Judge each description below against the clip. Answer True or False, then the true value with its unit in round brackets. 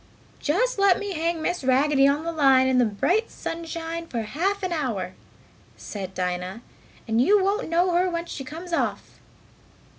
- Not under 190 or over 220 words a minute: False (170 wpm)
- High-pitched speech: True (320 Hz)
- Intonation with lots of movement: True (5.7 semitones)